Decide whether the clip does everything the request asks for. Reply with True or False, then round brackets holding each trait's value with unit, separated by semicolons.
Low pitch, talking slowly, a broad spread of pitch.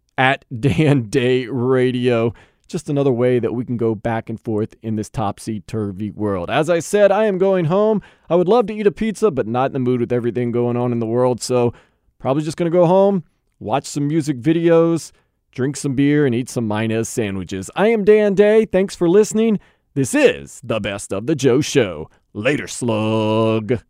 False (130 Hz; 205 wpm; 7.1 semitones)